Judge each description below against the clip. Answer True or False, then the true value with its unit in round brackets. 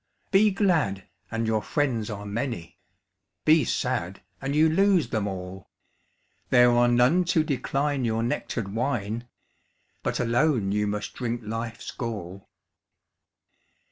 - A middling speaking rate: False (125 wpm)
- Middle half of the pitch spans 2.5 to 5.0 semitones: False (5.4 semitones)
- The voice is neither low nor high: False (120 Hz)